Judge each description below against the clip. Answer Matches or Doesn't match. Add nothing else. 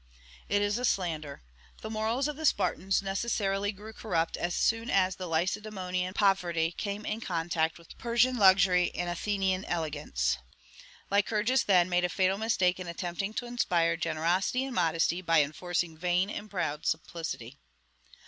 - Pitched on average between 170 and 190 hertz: Matches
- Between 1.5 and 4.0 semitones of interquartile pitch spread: Matches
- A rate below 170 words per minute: Matches